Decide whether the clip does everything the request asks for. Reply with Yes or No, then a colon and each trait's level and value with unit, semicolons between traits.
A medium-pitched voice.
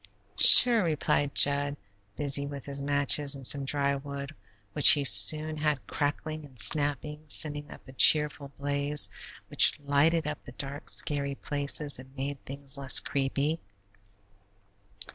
Yes: medium, 145 Hz